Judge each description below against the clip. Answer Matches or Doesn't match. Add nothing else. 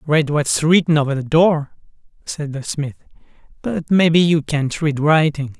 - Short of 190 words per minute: Matches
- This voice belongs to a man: Matches